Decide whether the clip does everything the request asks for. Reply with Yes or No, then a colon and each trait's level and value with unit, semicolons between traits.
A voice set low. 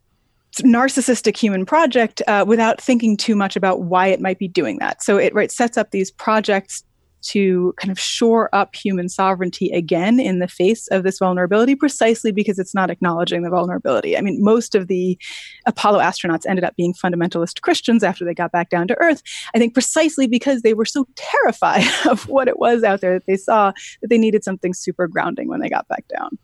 No: high, 200 Hz